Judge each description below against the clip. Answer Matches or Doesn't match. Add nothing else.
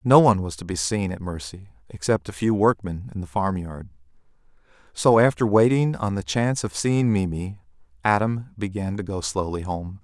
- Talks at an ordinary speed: Matches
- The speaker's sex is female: Doesn't match